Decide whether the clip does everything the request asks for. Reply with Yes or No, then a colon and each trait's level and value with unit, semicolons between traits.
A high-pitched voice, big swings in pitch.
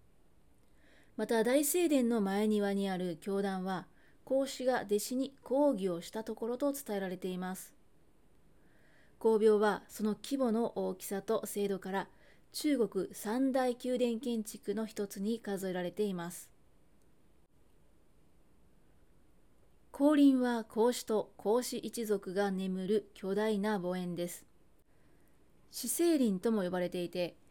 No: high, 215 Hz; average, 4.1 semitones